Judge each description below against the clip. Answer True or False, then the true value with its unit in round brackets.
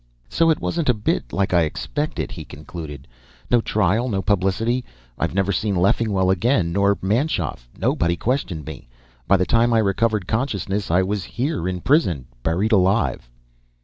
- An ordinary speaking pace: True (160 wpm)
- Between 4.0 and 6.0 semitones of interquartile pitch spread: True (4.5 semitones)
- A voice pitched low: True (100 Hz)